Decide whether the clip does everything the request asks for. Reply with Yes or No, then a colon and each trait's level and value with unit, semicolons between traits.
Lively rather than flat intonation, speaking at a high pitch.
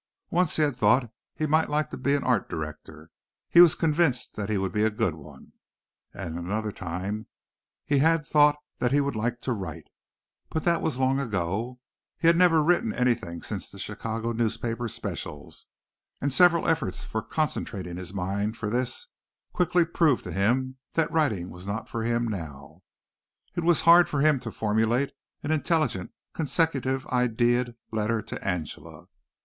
No: wide, 6.8 semitones; low, 120 Hz